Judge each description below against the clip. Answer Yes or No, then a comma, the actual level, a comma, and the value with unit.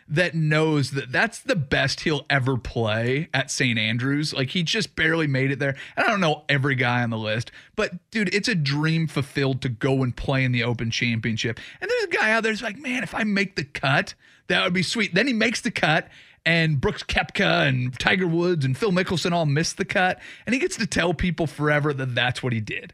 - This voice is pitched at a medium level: Yes, medium, 150 Hz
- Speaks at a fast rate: Yes, fast, 235 wpm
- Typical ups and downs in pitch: No, wide, 5.7 semitones